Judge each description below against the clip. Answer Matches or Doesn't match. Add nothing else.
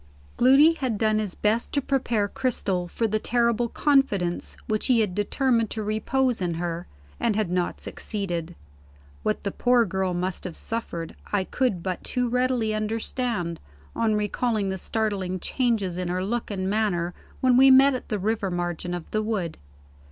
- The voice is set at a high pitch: Matches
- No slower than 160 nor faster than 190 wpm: Matches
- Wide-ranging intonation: Doesn't match